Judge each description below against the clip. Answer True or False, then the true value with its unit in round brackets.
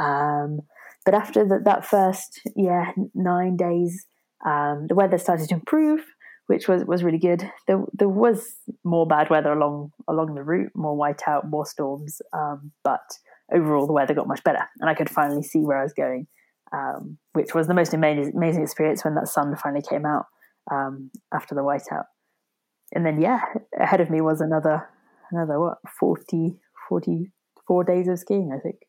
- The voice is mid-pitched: True (165 Hz)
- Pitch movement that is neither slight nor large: True (3.8 semitones)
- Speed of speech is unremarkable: True (180 wpm)